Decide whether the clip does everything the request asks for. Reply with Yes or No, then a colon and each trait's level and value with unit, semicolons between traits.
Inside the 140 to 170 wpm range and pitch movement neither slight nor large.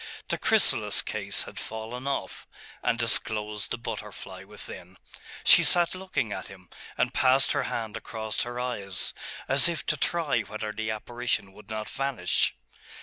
Yes: average, 150 wpm; average, 3.5 semitones